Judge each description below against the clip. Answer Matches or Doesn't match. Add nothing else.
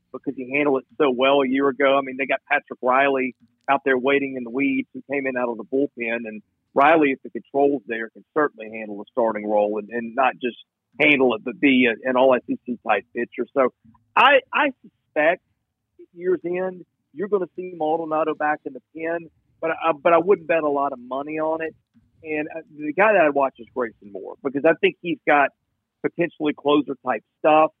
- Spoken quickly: Matches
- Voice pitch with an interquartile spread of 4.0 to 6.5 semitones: Matches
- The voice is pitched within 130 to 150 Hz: Matches